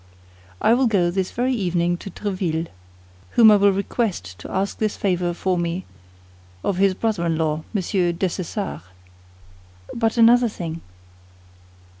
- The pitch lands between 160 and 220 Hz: Yes, high, 190 Hz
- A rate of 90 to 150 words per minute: Yes, average, 140 wpm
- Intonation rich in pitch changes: No, average, 3.7 semitones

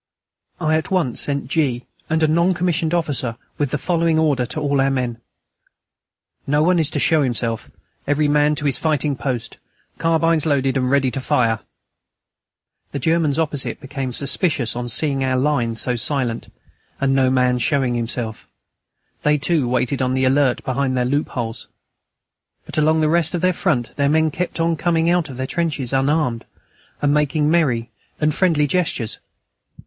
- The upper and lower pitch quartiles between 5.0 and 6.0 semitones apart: No, average, 3.8 semitones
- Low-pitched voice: No, medium, 145 Hz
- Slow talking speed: No, average, 170 wpm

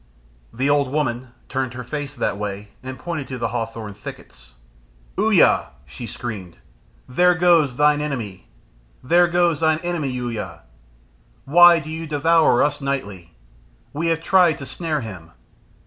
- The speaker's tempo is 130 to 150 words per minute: Yes, average, 145 wpm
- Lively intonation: Yes, wide, 5.8 semitones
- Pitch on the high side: No, medium, 140 Hz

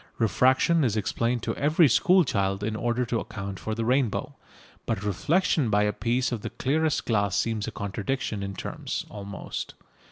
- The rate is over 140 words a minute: Yes, average, 170 wpm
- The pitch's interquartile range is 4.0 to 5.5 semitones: Yes, average, 4.4 semitones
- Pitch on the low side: Yes, low, 115 Hz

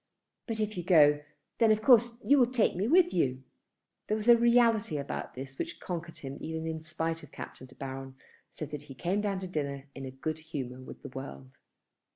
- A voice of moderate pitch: Yes, medium, 160 Hz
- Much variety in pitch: Yes, wide, 7.8 semitones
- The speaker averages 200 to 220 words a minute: Yes, fast, 205 wpm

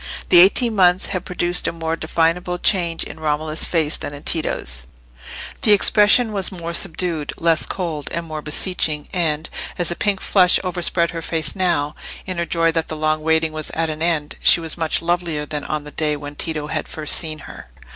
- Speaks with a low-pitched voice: No, medium, 165 Hz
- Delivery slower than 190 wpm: No, average, 195 wpm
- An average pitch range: No, narrow, 2.3 semitones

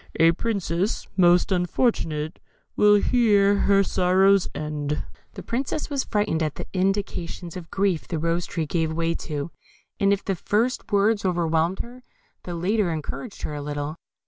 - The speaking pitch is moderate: Yes, medium, 180 Hz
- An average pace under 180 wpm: Yes, average, 155 wpm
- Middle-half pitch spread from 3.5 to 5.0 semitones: Yes, average, 3.8 semitones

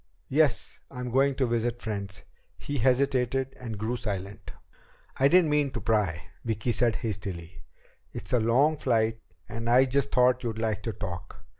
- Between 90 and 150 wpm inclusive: No, average, 160 wpm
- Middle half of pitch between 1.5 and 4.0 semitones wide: Yes, average, 3.5 semitones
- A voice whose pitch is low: Yes, low, 120 Hz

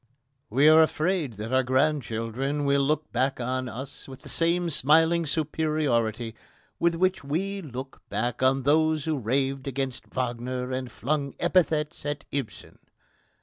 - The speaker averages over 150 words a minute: No, average, 140 wpm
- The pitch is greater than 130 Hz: Yes, medium, 140 Hz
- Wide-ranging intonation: No, average, 3.6 semitones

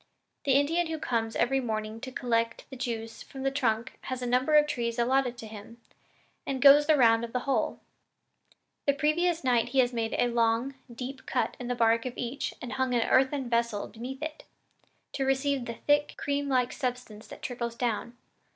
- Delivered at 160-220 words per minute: Yes, average, 190 wpm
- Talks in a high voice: Yes, very high, 250 Hz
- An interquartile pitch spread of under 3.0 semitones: Yes, narrow, 2.6 semitones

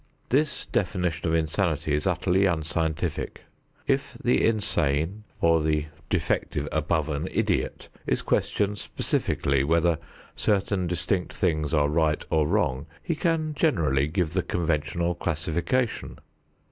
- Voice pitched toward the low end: Yes, very low, 80 Hz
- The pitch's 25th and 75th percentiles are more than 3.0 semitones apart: Yes, average, 3.8 semitones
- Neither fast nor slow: No, slow, 120 wpm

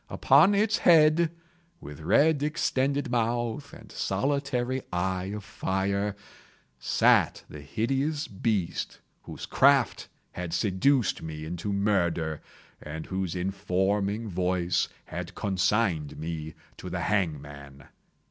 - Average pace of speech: No, slow, 110 wpm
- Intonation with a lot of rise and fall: Yes, wide, 6.9 semitones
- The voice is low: Yes, low, 100 Hz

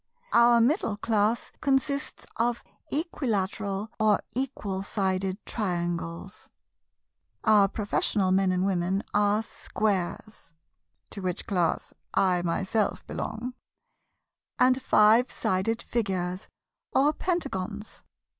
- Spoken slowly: Yes, slow, 95 wpm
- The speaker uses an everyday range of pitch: Yes, average, 3.7 semitones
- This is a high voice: Yes, high, 205 Hz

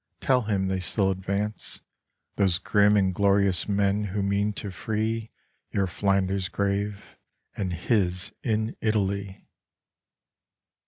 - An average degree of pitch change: No, narrow, 1.5 semitones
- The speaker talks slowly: Yes, slow, 115 wpm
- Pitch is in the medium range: No, low, 100 Hz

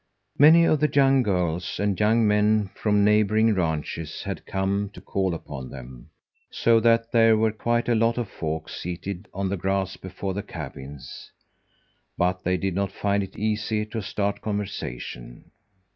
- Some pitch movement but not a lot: Yes, average, 3.4 semitones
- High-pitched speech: No, low, 100 Hz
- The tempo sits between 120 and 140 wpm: No, average, 160 wpm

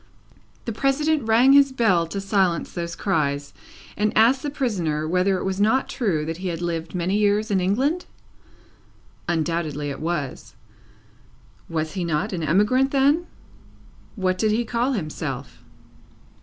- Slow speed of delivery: No, average, 145 wpm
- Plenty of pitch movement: Yes, wide, 6.1 semitones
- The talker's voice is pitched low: No, high, 195 Hz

